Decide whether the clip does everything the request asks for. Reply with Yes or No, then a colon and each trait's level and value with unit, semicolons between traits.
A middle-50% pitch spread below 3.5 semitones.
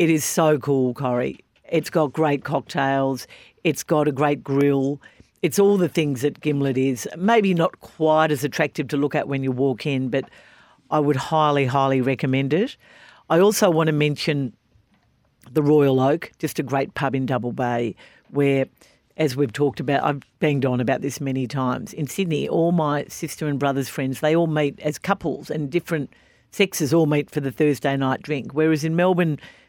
Yes: narrow, 2.6 semitones